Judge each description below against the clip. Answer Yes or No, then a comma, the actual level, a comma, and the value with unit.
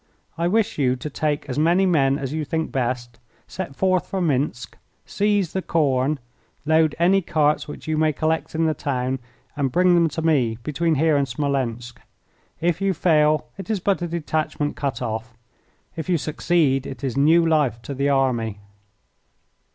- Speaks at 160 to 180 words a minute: Yes, average, 175 wpm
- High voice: No, medium, 150 Hz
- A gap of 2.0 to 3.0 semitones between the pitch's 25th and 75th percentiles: No, average, 3.9 semitones